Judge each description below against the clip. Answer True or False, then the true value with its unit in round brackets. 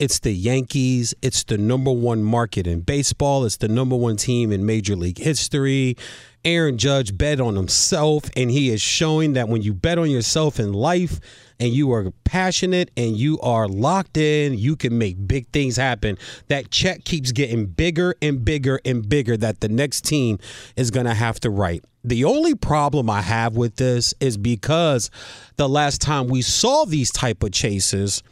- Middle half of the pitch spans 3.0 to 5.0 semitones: True (4.4 semitones)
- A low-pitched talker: True (125 Hz)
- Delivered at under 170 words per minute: False (185 wpm)